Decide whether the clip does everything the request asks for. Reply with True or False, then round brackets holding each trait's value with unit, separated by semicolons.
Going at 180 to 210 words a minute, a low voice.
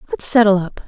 False (205 wpm; 200 Hz)